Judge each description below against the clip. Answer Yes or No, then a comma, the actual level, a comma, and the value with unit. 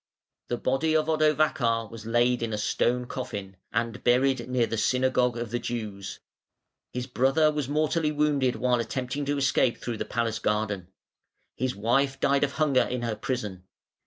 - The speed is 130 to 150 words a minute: No, average, 165 wpm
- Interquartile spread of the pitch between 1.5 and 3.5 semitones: Yes, average, 3.1 semitones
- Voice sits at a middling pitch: No, low, 125 Hz